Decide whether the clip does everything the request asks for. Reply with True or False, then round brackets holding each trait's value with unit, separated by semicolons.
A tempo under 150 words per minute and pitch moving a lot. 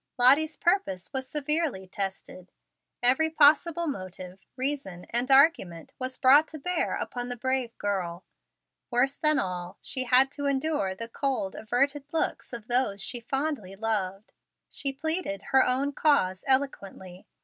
True (140 wpm; 6.5 semitones)